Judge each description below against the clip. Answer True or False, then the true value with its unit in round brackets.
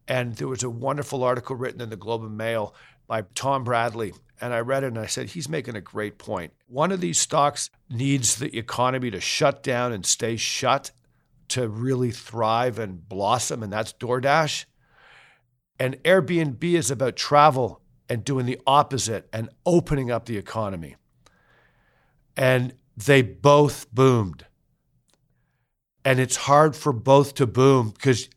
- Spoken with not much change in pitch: False (3.2 semitones)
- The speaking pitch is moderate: False (125 Hz)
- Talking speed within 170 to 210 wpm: False (155 wpm)